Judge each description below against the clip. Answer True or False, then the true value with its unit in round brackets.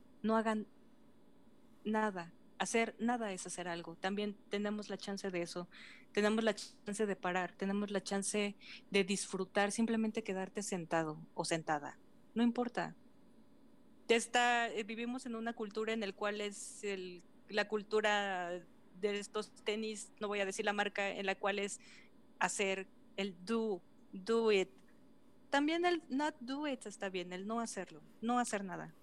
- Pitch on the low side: False (215 Hz)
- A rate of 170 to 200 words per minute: False (155 wpm)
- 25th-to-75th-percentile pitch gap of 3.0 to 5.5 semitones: True (3.8 semitones)